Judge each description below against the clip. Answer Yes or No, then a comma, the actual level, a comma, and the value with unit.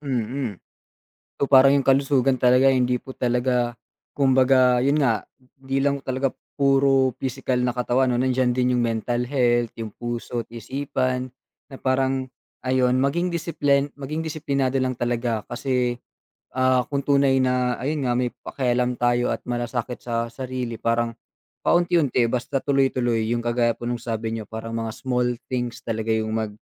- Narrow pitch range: Yes, narrow, 2.0 semitones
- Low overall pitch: Yes, low, 125 Hz